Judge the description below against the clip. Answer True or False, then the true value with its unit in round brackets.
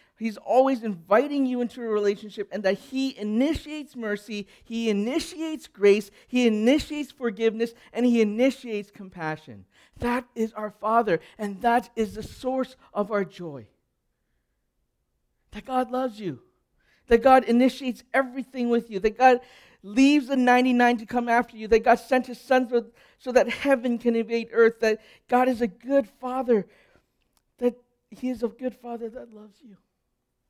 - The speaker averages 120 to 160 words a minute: True (155 wpm)